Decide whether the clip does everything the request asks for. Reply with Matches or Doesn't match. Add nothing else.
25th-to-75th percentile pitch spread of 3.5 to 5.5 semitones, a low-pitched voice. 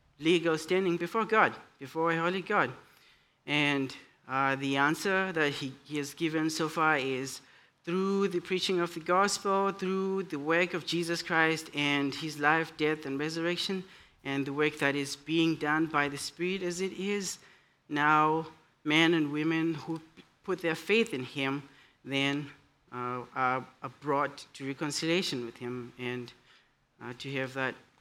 Doesn't match